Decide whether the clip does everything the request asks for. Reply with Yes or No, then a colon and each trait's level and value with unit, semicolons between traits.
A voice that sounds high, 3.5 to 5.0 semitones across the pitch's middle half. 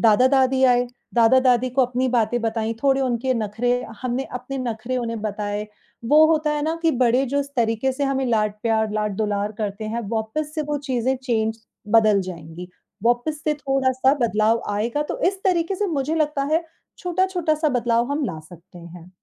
Yes: high, 245 Hz; average, 4.0 semitones